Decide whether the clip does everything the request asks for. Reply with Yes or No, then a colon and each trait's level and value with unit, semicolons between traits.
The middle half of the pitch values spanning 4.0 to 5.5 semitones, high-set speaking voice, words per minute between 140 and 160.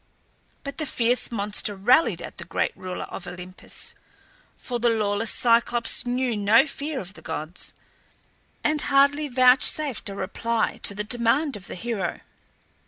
Yes: average, 4.4 semitones; high, 235 Hz; average, 150 wpm